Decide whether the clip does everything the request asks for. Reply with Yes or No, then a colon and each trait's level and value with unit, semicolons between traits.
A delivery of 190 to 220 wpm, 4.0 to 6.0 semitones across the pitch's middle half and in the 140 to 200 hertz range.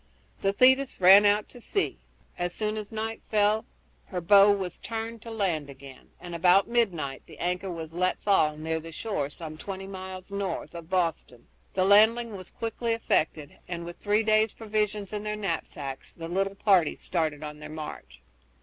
No: average, 175 wpm; average, 4.5 semitones; high, 190 Hz